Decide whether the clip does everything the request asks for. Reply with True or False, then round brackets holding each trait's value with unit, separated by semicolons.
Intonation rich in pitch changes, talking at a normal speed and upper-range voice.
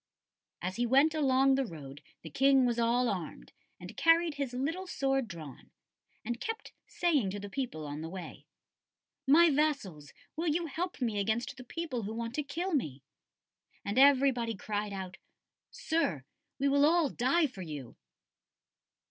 True (6.5 semitones; 160 wpm; 255 Hz)